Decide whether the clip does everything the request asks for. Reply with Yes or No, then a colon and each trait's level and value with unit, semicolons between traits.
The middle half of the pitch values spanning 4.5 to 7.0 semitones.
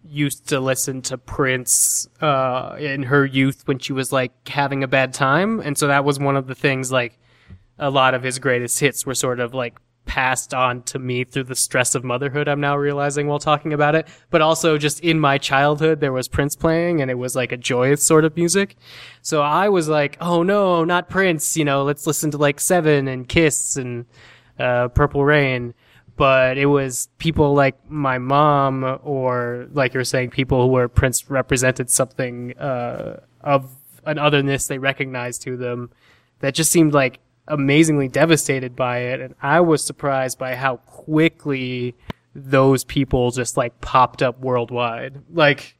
No: narrow, 2.5 semitones